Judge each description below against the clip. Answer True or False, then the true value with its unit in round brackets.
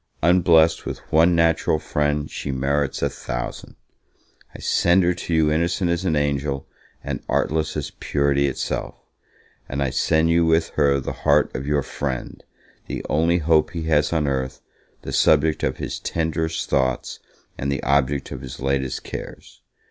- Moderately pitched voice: False (75 Hz)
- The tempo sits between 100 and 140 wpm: False (165 wpm)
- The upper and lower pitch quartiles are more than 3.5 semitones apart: False (2.9 semitones)